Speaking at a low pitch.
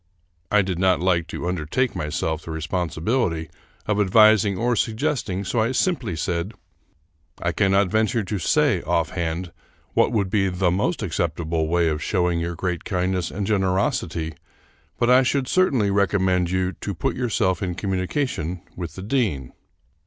Yes: very low, 95 Hz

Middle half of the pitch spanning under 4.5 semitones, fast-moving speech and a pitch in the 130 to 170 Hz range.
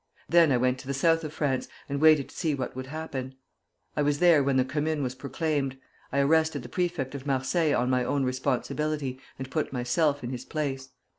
Yes: average, 2.9 semitones; fast, 210 wpm; medium, 140 Hz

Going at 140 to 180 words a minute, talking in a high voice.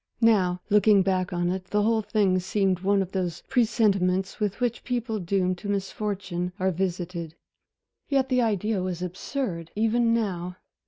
Yes: average, 155 wpm; high, 195 Hz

